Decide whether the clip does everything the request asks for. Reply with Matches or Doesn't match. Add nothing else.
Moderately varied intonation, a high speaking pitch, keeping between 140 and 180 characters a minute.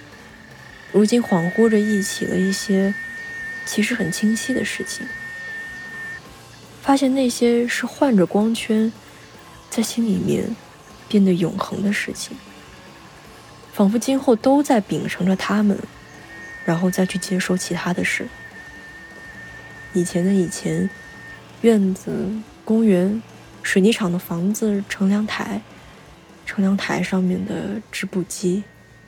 Matches